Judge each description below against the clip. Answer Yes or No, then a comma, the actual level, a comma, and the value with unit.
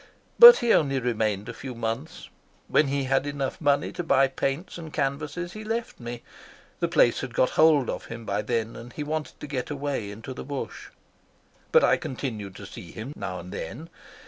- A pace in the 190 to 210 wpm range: Yes, average, 200 wpm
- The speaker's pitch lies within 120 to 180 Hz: Yes, low, 135 Hz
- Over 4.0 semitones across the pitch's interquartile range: Yes, average, 4.5 semitones